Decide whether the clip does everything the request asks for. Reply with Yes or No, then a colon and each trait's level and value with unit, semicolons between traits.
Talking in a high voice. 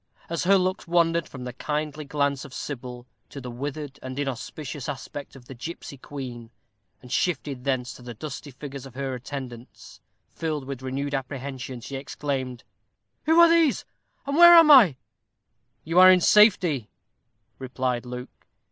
No: medium, 140 Hz